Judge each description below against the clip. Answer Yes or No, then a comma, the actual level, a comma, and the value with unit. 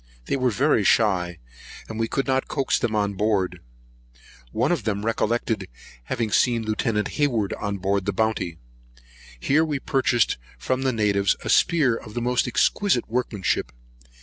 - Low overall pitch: Yes, low, 110 Hz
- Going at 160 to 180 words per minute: No, average, 150 wpm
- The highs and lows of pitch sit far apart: No, average, 3.9 semitones